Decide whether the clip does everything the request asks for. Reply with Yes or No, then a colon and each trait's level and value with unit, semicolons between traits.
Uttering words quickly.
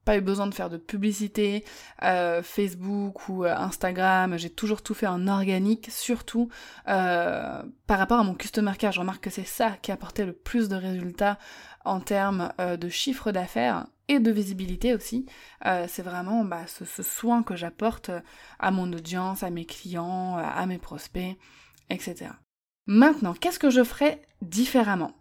No: average, 175 wpm